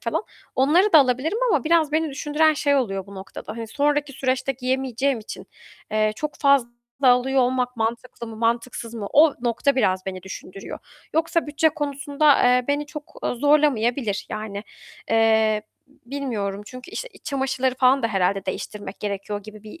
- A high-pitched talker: Yes, very high, 255 Hz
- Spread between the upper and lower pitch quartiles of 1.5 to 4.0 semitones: No, average, 4.7 semitones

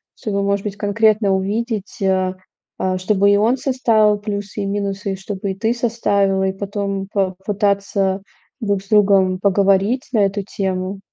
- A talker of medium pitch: No, high, 200 Hz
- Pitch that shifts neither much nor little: No, narrow, 1.4 semitones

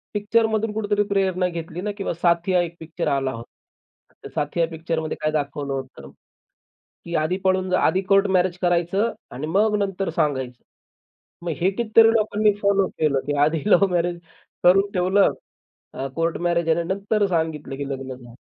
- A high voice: No, medium, 175 Hz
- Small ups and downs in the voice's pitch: No, average, 4.2 semitones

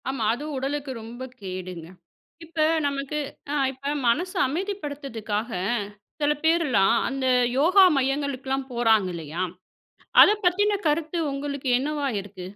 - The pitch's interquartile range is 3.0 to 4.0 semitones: No, average, 4.8 semitones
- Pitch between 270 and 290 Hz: Yes, very high, 275 Hz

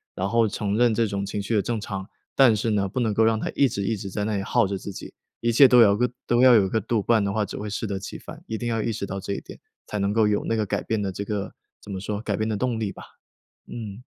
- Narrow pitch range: Yes, narrow, 2.3 semitones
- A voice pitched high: No, low, 105 Hz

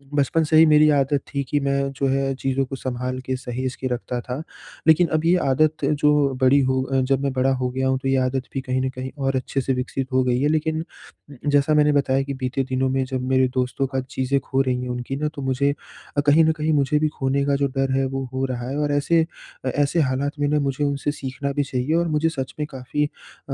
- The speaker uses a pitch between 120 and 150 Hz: Yes, low, 135 Hz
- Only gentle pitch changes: Yes, narrow, 1.9 semitones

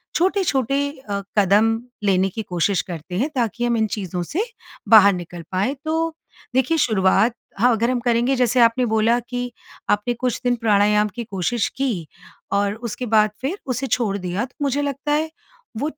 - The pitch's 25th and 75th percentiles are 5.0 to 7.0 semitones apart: No, average, 4.1 semitones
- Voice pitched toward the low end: No, high, 230 Hz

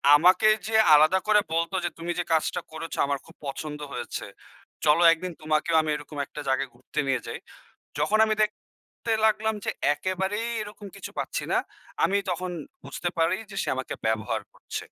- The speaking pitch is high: No, medium, 165 Hz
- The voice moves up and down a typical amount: Yes, average, 4.7 semitones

